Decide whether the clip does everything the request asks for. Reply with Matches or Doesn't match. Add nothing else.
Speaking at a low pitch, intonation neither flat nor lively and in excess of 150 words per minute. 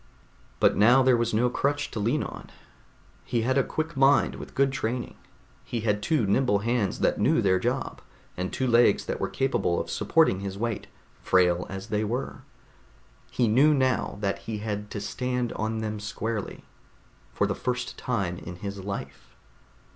Matches